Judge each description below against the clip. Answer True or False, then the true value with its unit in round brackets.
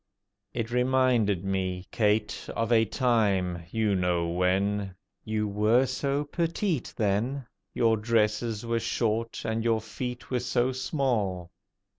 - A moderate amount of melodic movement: True (3.5 semitones)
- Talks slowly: True (120 wpm)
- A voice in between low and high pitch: False (110 Hz)